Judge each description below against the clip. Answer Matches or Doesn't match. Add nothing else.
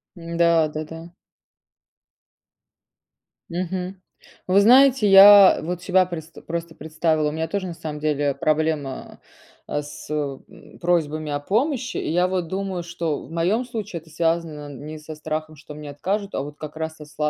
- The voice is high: Doesn't match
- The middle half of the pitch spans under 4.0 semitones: Matches